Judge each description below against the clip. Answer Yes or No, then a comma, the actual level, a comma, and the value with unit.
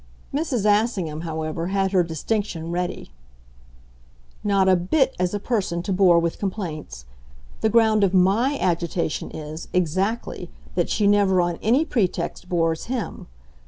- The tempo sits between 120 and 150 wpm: Yes, average, 140 wpm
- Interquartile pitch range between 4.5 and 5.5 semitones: No, average, 4.0 semitones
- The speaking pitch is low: No, medium, 185 Hz